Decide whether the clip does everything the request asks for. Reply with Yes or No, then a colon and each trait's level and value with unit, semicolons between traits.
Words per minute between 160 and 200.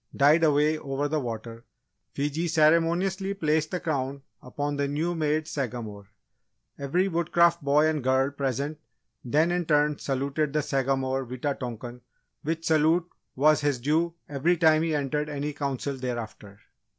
No: average, 145 wpm